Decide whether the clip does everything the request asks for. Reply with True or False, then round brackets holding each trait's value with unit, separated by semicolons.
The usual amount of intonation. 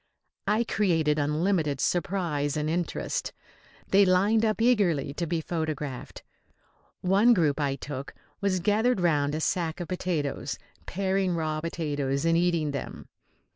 True (4.2 semitones)